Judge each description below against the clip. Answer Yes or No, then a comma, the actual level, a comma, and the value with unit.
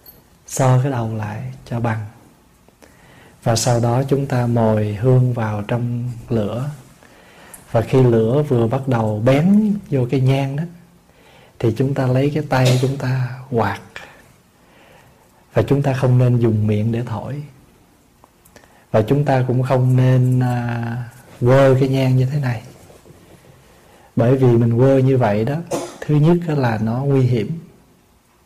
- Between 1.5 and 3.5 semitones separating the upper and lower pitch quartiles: Yes, average, 2.7 semitones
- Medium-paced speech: No, slow, 150 wpm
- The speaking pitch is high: No, low, 125 Hz